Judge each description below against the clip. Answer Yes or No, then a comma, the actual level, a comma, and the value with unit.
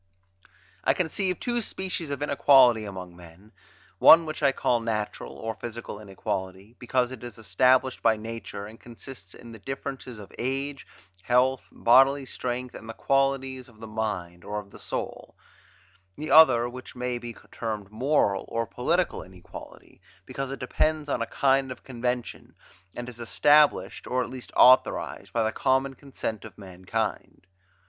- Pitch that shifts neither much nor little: Yes, average, 3.6 semitones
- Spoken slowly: No, average, 155 wpm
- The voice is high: No, low, 120 Hz